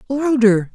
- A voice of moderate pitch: No, high, 240 Hz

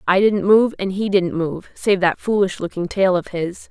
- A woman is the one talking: Yes, female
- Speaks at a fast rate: Yes, fast, 225 wpm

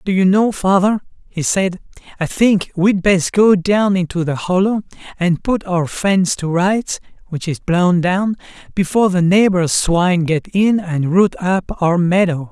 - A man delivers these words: Yes, male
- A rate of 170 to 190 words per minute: Yes, average, 175 wpm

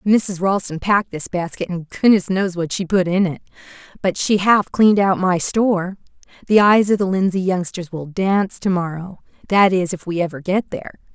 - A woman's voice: Yes, female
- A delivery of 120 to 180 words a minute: No, average, 190 wpm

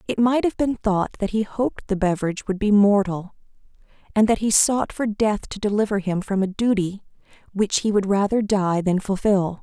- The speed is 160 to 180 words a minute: No, average, 200 wpm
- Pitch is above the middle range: Yes, high, 205 Hz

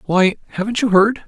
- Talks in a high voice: Yes, high, 205 Hz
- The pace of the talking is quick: No, average, 190 wpm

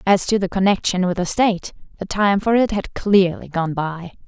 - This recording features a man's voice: No, female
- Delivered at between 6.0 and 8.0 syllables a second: No, 5.0 syllables/s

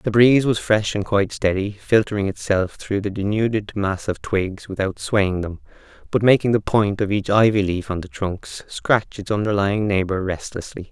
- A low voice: Yes, low, 100 Hz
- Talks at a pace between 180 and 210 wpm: Yes, average, 185 wpm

